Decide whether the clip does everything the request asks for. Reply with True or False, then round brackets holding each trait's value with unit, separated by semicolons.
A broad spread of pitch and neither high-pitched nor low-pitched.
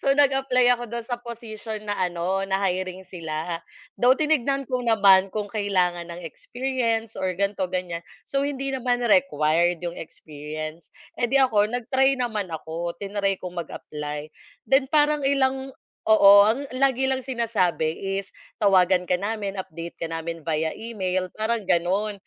False (6.0 semitones; 205 Hz)